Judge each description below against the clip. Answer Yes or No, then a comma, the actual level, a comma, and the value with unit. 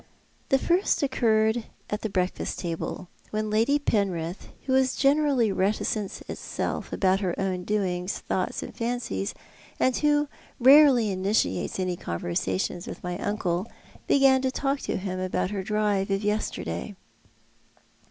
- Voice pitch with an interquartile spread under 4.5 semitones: No, wide, 5.6 semitones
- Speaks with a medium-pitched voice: No, high, 210 Hz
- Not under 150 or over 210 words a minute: No, slow, 135 wpm